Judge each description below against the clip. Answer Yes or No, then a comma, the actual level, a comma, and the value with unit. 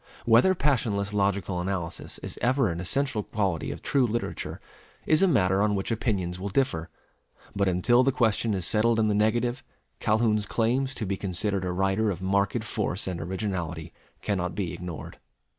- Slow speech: No, average, 170 wpm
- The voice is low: Yes, low, 100 Hz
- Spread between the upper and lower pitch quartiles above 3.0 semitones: Yes, average, 3.8 semitones